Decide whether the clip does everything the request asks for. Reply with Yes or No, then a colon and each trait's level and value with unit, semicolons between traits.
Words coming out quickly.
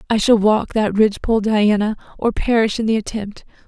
No: average, 180 wpm